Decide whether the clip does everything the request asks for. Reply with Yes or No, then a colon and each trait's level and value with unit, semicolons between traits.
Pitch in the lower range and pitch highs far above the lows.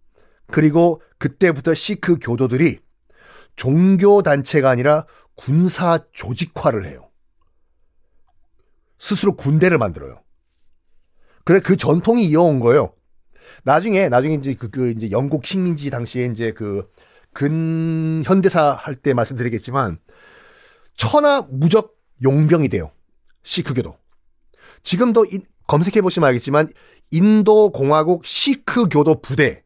No: medium, 155 Hz; wide, 6.5 semitones